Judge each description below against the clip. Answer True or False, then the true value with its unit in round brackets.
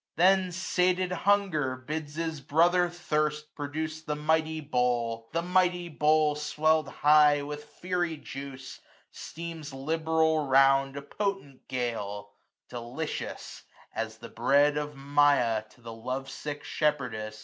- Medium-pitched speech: True (150 Hz)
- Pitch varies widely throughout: False (3.3 semitones)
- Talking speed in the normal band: False (130 wpm)